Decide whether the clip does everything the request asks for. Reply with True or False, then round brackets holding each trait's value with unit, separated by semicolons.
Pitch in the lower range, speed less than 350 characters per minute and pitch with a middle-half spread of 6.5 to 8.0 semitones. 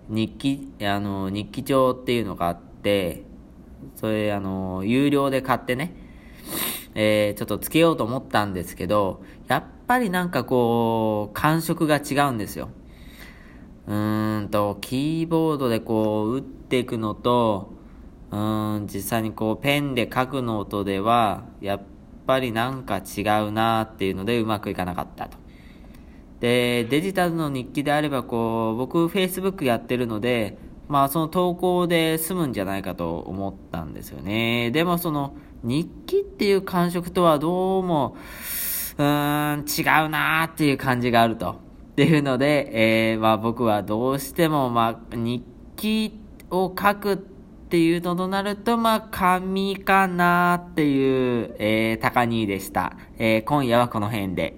True (125 Hz; 295 characters per minute; 6.9 semitones)